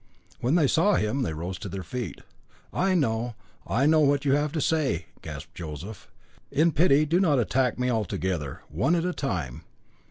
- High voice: No, low, 135 Hz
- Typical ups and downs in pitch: No, wide, 7.1 semitones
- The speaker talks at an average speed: Yes, average, 190 wpm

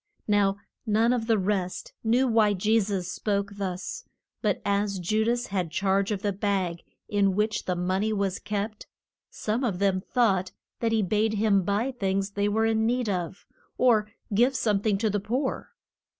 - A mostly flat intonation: Yes, narrow, 2.2 semitones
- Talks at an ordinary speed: Yes, average, 180 wpm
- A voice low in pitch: No, high, 205 Hz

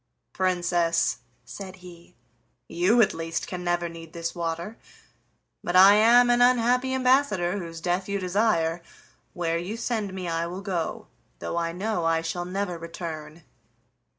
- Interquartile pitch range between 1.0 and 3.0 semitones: No, average, 3.4 semitones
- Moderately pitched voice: Yes, medium, 180 Hz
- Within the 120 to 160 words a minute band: Yes, average, 150 wpm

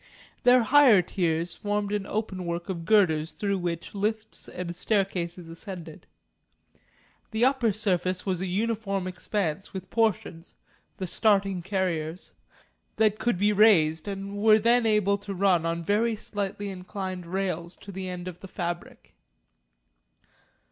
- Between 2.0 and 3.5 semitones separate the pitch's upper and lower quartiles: Yes, average, 3.0 semitones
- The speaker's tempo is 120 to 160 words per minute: Yes, slow, 135 wpm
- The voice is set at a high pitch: Yes, high, 195 Hz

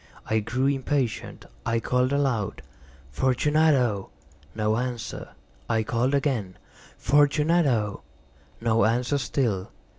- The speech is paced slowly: Yes, slow, 95 wpm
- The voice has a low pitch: Yes, low, 125 Hz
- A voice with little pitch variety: No, average, 4.0 semitones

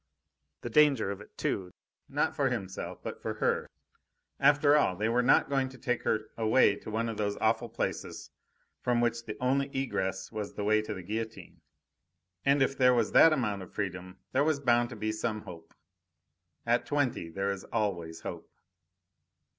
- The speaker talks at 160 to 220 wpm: Yes, average, 180 wpm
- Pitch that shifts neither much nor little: Yes, average, 4.1 semitones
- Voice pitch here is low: Yes, low, 115 Hz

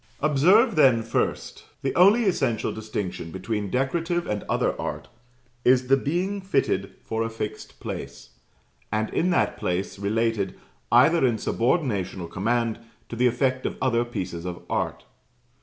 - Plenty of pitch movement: Yes, wide, 5.7 semitones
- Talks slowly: No, average, 145 wpm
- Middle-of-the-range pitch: No, low, 120 Hz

